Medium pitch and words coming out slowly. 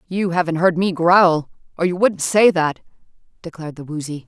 No: medium, 170 Hz; average, 180 wpm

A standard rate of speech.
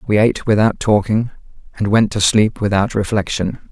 Yes: average, 160 wpm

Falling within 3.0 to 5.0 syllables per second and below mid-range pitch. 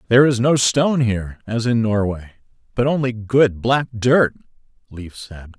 Yes: 4.8 syllables/s; low, 115 Hz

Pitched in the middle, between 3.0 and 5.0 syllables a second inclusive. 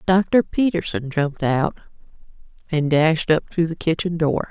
Yes: medium, 165 Hz; 4.3 syllables/s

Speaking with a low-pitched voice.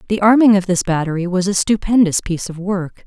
No: high, 190 Hz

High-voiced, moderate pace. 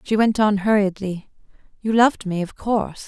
Yes: high, 205 Hz; average, 175 wpm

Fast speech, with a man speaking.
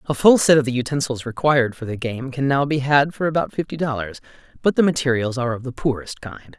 Yes: fast, 235 wpm; male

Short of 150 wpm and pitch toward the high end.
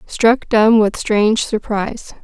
Yes: slow, 135 wpm; high, 220 Hz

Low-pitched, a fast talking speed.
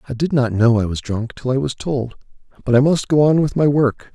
Yes: low, 130 Hz; fast, 275 wpm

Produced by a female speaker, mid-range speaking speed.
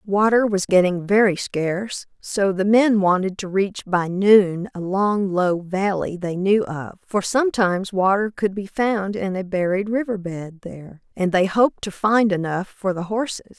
Yes: female; average, 180 wpm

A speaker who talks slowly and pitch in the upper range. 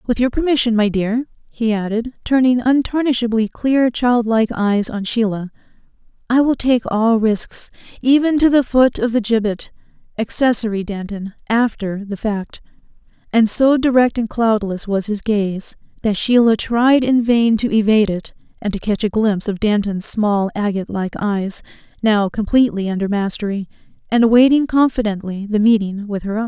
No: average, 155 wpm; high, 225 Hz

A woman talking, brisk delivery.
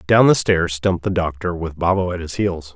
No: male; fast, 240 wpm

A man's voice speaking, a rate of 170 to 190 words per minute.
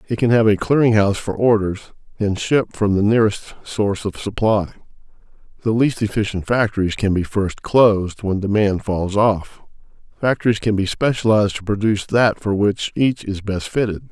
Yes: male; average, 175 wpm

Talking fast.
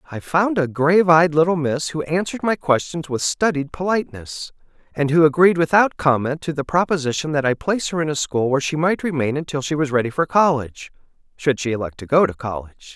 Yes: fast, 210 wpm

